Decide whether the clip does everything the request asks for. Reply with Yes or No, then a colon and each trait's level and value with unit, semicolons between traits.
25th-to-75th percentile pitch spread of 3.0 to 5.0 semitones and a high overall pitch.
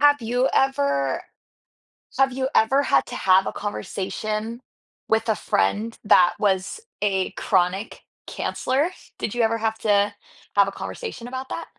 Yes: average, 4.6 semitones; high, 220 Hz